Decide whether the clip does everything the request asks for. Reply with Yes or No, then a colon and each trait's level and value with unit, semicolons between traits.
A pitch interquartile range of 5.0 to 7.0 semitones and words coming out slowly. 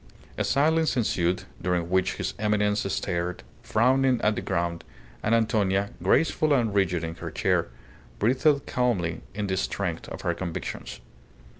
No: wide, 5.5 semitones; average, 145 wpm